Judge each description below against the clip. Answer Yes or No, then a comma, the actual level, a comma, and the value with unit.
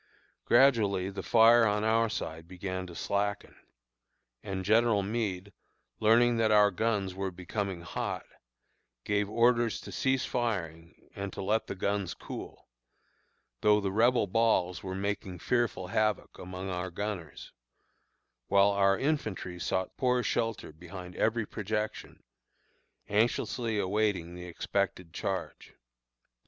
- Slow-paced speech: Yes, slow, 125 wpm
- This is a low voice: Yes, low, 100 Hz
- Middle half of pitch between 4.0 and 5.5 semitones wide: No, average, 3.3 semitones